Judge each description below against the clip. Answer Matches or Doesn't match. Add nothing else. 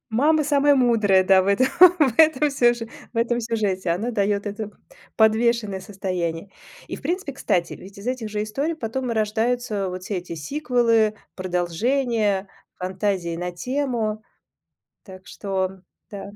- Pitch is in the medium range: Doesn't match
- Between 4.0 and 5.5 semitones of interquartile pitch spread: Matches